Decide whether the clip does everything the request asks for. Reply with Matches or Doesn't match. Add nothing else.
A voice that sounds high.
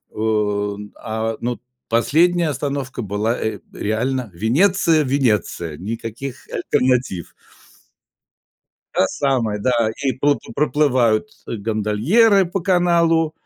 Doesn't match